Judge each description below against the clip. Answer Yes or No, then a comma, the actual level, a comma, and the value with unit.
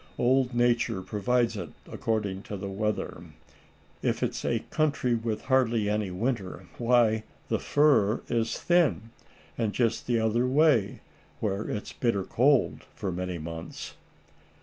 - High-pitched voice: No, low, 115 Hz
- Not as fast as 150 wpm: Yes, slow, 135 wpm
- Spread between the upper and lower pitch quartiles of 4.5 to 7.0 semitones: No, average, 3.5 semitones